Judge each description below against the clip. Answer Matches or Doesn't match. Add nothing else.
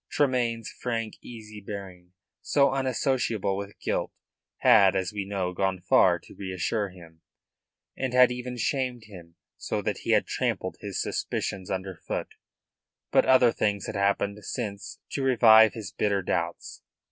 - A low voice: Matches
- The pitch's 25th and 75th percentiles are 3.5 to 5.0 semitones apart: Matches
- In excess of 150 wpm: Doesn't match